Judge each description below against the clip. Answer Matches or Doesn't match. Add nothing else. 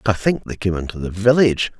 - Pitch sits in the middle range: Doesn't match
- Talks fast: Matches